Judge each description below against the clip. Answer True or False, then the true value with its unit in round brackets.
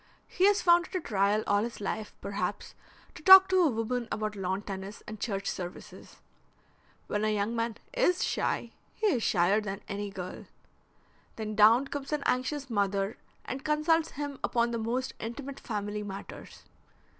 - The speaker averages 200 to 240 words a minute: False (165 wpm)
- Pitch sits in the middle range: False (225 Hz)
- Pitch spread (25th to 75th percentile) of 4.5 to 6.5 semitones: True (5.5 semitones)